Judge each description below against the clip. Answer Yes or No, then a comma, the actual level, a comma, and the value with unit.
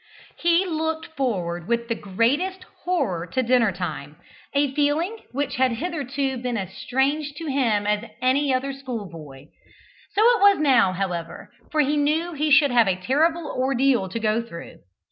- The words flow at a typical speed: Yes, average, 165 wpm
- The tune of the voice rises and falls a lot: Yes, wide, 6.1 semitones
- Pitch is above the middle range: Yes, very high, 260 Hz